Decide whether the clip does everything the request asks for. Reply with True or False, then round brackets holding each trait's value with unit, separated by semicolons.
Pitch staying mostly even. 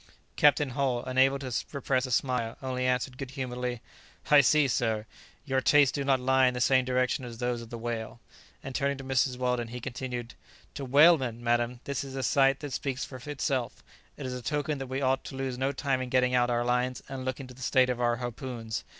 True (1.6 semitones)